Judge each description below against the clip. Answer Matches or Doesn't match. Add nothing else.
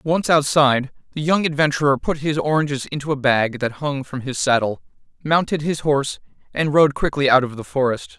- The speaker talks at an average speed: Matches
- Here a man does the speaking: Matches